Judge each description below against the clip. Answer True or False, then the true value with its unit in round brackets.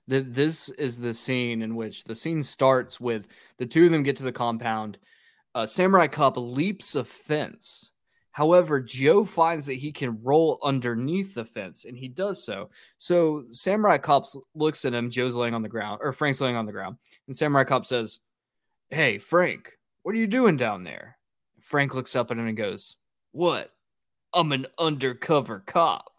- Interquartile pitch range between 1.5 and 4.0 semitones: False (4.8 semitones)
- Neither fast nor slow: True (180 wpm)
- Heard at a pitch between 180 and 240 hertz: False (135 Hz)